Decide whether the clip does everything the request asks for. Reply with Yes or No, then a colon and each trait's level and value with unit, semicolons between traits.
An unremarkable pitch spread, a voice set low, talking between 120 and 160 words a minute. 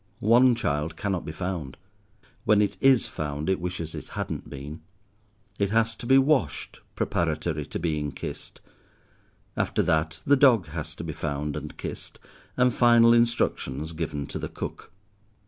No: wide, 7.3 semitones; very low, 85 Hz; average, 155 wpm